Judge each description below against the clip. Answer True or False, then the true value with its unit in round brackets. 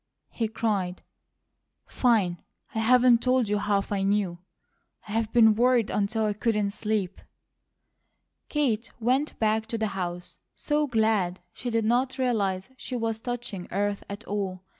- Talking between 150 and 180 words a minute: False (140 wpm)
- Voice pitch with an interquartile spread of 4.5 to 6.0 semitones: False (3.1 semitones)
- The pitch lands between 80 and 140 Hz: False (220 Hz)